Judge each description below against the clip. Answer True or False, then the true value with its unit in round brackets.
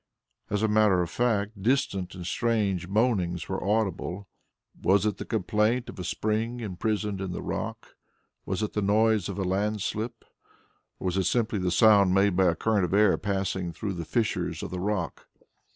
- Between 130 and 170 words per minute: False (185 wpm)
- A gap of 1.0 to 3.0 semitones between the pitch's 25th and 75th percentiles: True (2.7 semitones)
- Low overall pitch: True (100 Hz)